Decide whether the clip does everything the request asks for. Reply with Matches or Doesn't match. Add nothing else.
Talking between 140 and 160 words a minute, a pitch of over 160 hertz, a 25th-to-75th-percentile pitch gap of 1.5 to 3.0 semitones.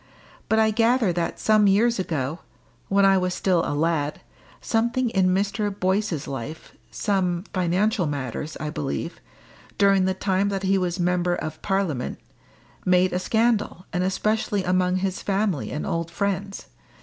Matches